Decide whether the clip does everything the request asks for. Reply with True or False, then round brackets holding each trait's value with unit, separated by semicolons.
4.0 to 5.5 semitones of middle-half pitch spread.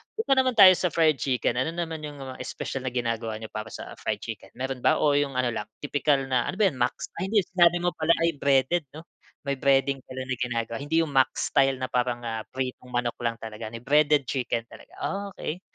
True (4.3 semitones)